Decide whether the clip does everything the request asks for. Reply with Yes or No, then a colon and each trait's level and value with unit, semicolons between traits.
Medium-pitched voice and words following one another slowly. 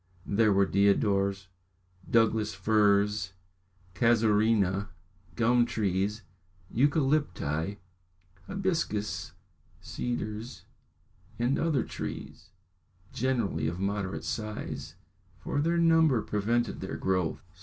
No: low, 105 Hz; slow, 85 wpm